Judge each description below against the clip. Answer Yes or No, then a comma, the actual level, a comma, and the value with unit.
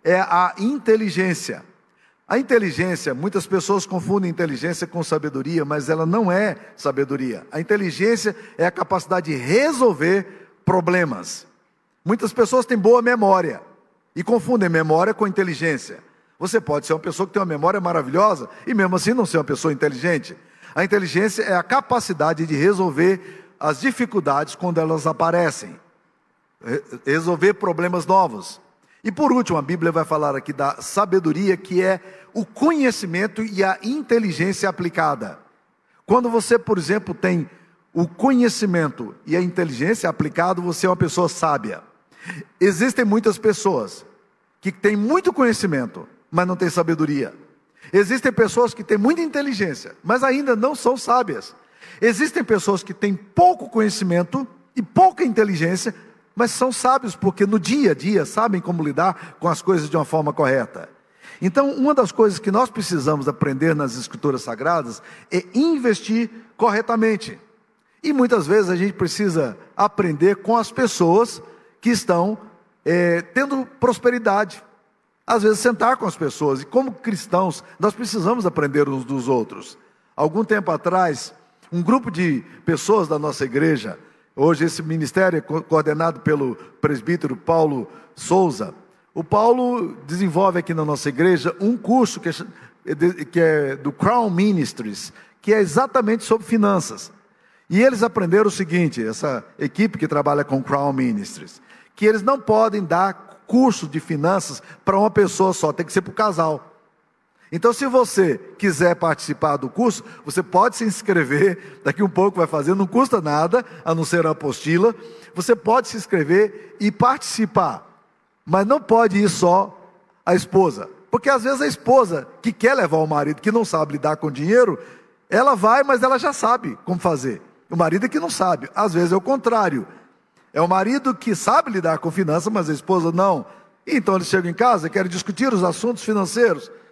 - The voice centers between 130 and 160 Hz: No, high, 190 Hz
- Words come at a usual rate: Yes, average, 160 wpm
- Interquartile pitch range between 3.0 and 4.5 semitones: No, average, 5.2 semitones